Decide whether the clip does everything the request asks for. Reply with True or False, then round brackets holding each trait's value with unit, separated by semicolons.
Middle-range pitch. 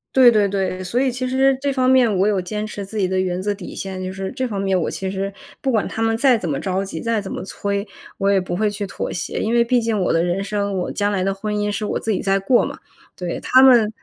False (205 Hz)